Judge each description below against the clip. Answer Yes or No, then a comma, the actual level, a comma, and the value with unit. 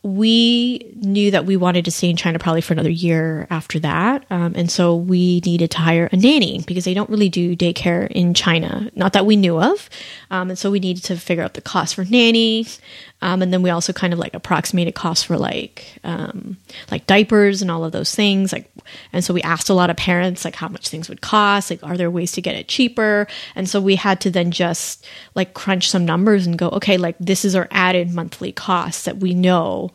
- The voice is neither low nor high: Yes, medium, 180 Hz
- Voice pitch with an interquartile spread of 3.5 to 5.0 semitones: No, narrow, 2.5 semitones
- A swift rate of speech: Yes, fast, 230 wpm